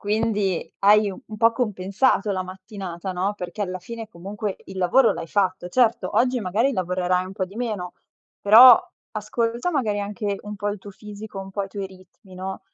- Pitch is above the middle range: Yes, high, 200 Hz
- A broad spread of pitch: No, average, 2.7 semitones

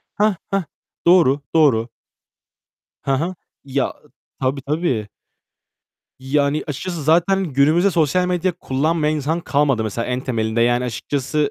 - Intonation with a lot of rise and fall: No, average, 4.5 semitones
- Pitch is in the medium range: Yes, medium, 145 Hz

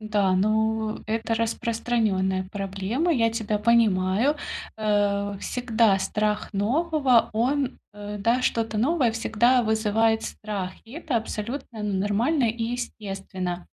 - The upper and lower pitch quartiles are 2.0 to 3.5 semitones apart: Yes, narrow, 2.5 semitones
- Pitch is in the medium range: No, high, 220 Hz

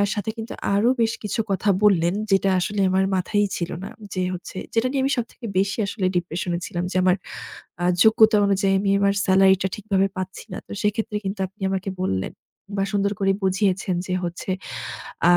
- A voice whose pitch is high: Yes, high, 195 Hz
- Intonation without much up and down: Yes, narrow, 1.9 semitones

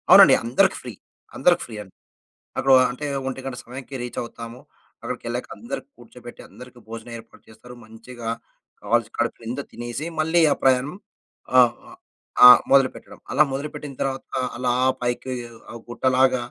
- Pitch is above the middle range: No, low, 125 Hz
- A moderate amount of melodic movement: No, narrow, 2.2 semitones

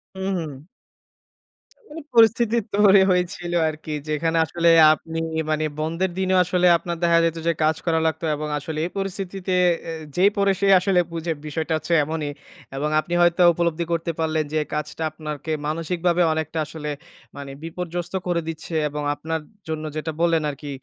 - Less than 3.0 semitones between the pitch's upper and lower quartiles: Yes, narrow, 2.4 semitones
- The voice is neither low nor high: Yes, medium, 165 Hz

